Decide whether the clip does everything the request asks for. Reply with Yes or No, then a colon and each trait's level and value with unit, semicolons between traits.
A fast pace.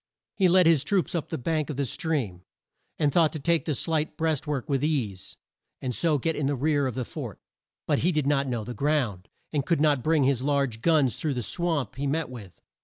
Yes: fast, 230 wpm